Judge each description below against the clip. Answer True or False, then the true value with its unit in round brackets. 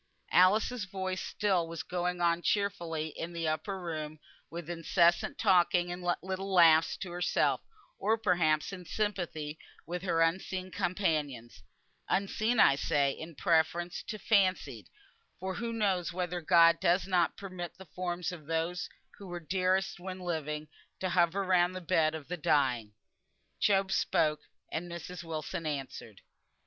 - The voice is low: False (175 Hz)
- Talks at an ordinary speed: True (145 wpm)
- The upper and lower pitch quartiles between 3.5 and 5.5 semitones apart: False (2.6 semitones)